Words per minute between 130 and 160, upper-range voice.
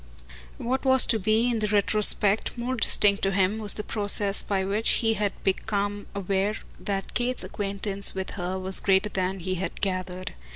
No: average, 175 wpm; high, 200 Hz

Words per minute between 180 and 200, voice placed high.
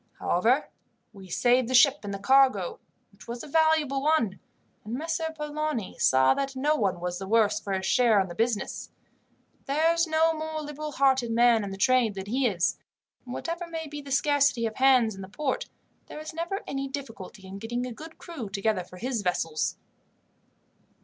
Yes: average, 190 wpm; very high, 250 Hz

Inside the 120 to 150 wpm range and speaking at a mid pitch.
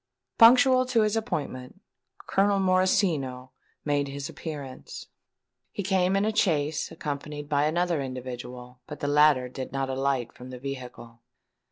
Yes: average, 140 wpm; medium, 145 Hz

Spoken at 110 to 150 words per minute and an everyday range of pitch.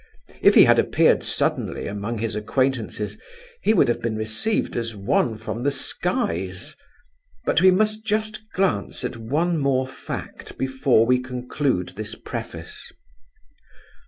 Yes: slow, 135 wpm; average, 4.8 semitones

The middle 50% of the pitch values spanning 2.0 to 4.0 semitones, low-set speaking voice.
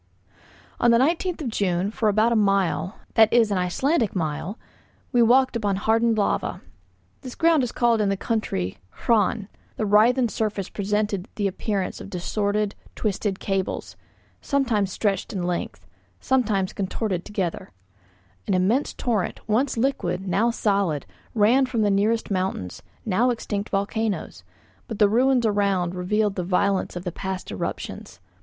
No: average, 3.3 semitones; high, 205 Hz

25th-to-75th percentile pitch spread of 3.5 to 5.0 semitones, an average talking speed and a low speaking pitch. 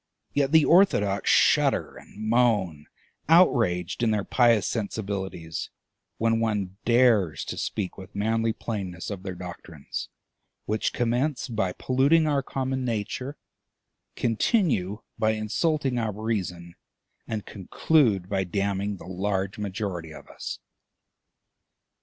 No: average, 4.2 semitones; slow, 115 wpm; low, 105 Hz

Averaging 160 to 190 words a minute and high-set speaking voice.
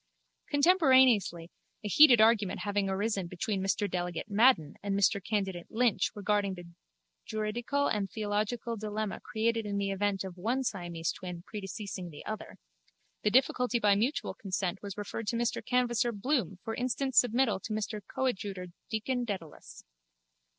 No: average, 145 wpm; high, 210 Hz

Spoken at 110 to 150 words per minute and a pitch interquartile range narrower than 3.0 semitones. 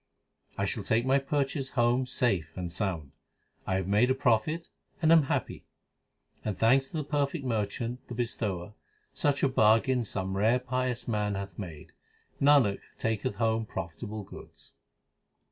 No: average, 145 wpm; average, 4.5 semitones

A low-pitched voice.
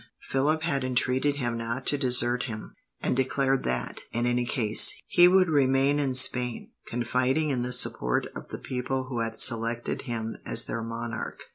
Yes: low, 125 Hz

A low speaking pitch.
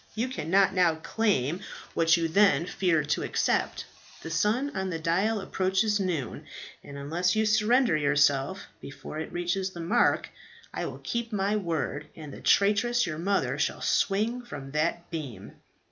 No: medium, 180 Hz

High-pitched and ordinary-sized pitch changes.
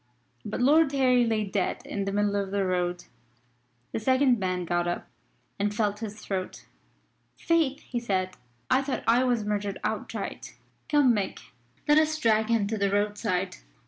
Yes: high, 210 Hz; average, 4.2 semitones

